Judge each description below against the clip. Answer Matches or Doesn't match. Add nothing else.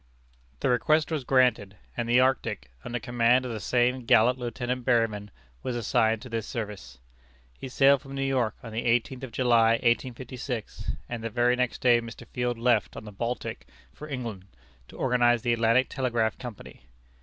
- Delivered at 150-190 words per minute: Matches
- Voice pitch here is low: Matches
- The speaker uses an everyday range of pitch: Doesn't match